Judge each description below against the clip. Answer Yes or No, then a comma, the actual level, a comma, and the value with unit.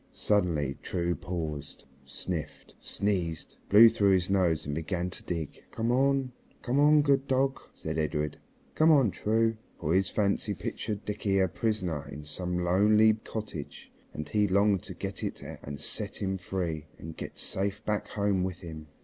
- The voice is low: Yes, very low, 95 Hz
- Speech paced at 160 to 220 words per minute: Yes, average, 165 wpm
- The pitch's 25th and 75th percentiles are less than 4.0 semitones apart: No, average, 4.8 semitones